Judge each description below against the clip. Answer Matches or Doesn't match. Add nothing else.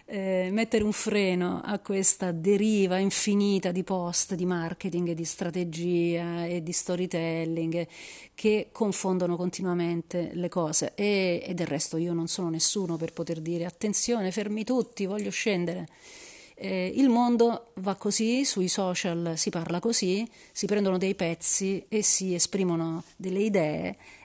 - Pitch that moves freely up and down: Doesn't match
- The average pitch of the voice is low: Doesn't match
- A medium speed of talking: Matches